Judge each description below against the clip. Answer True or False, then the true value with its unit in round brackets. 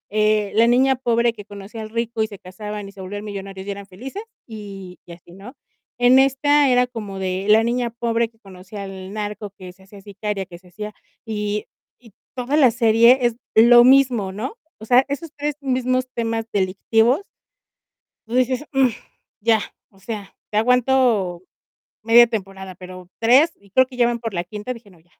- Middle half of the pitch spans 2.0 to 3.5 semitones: False (3.9 semitones)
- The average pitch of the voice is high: True (220 Hz)